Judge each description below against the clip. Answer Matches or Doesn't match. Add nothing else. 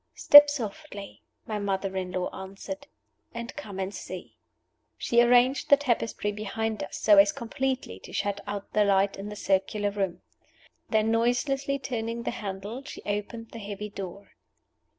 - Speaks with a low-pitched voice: Doesn't match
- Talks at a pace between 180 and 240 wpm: Doesn't match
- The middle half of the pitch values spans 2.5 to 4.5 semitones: Matches